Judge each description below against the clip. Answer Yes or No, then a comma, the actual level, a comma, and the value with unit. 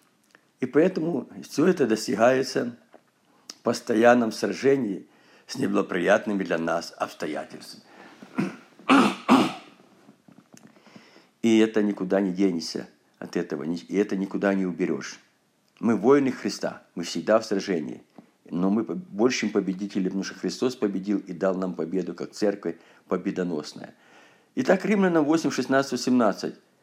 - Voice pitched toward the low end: Yes, low, 100 Hz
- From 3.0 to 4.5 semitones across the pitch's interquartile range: Yes, average, 4.2 semitones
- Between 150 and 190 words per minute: No, average, 115 wpm